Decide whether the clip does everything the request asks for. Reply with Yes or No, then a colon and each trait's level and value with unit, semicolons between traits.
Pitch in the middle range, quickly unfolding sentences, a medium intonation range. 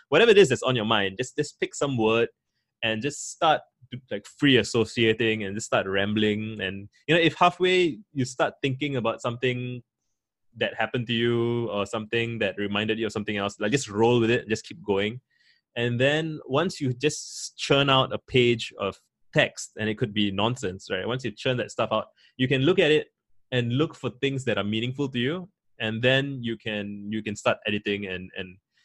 No: low, 120 Hz; fast, 210 wpm; average, 3.6 semitones